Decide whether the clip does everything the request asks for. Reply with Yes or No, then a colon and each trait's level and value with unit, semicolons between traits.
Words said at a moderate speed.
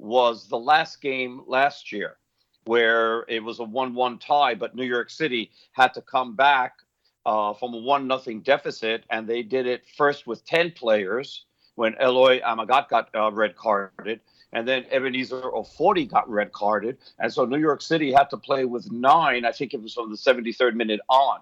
Yes: average, 185 wpm